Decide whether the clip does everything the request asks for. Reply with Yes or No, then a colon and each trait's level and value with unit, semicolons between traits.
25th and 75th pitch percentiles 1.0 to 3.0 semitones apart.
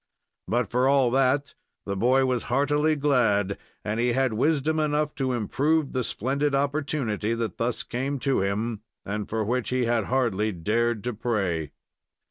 No: average, 4.1 semitones